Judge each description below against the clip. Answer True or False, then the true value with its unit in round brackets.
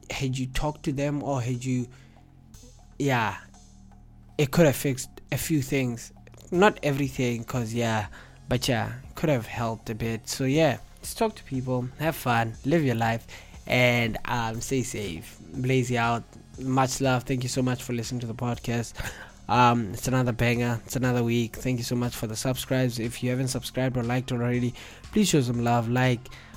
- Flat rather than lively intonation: True (2.0 semitones)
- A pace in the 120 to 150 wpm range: False (185 wpm)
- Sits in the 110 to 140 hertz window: True (125 Hz)